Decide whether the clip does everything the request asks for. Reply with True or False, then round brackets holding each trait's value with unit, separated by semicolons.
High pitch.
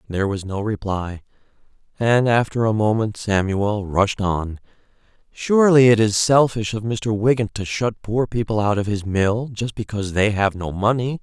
False (110 Hz)